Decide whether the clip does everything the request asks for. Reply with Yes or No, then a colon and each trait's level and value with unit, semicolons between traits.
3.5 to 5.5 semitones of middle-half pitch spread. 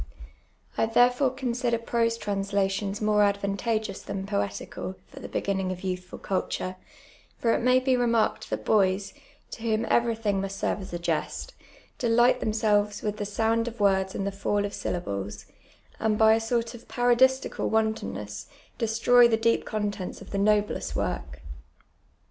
No: average, 2.8 semitones